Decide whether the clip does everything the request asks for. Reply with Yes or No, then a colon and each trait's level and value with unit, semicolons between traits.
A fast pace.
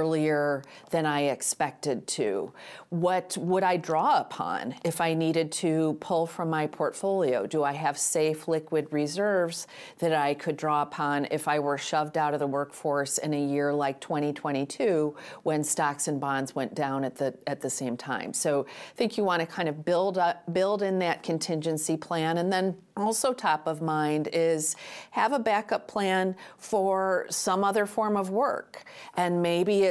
No: average, 180 wpm